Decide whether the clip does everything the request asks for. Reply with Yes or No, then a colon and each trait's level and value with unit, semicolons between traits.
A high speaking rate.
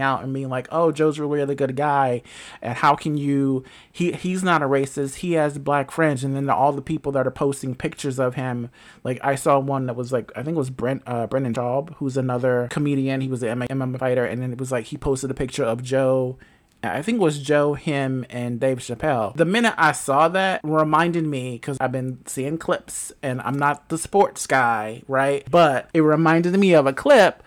Yes: fast, 225 wpm